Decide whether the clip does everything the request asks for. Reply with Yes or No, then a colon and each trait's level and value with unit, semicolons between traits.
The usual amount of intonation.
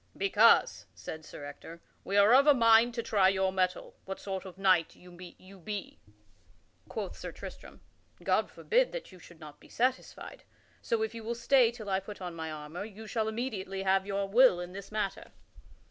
Yes: average, 3.6 semitones